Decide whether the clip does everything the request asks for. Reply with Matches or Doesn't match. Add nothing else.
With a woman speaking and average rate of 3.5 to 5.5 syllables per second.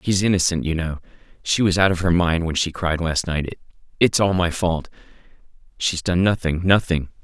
Doesn't match